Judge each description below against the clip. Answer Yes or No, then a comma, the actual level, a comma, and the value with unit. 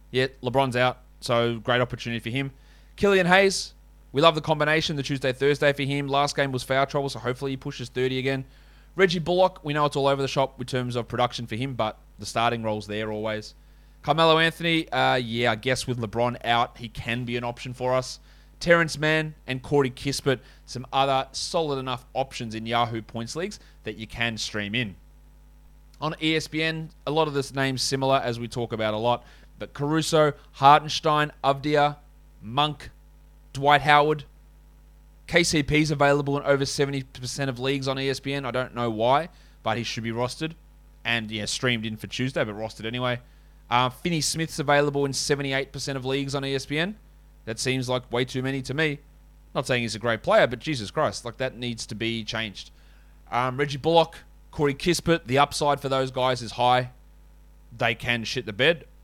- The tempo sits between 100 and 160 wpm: No, average, 185 wpm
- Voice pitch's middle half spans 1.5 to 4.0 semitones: Yes, average, 3.4 semitones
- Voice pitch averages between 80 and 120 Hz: No, low, 135 Hz